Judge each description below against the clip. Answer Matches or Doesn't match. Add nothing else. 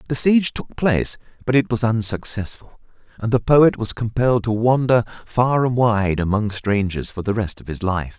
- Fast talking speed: Doesn't match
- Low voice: Matches